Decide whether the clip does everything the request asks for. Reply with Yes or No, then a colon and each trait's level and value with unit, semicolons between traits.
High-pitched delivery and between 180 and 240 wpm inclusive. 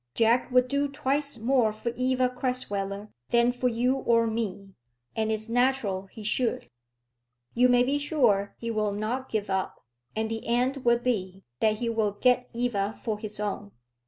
No: high, 230 Hz; average, 170 wpm